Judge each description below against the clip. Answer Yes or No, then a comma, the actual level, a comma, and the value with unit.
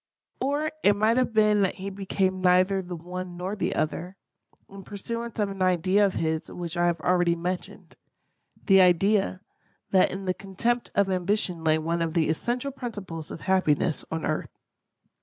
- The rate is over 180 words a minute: No, average, 170 wpm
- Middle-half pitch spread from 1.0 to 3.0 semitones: Yes, average, 2.7 semitones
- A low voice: No, medium, 185 Hz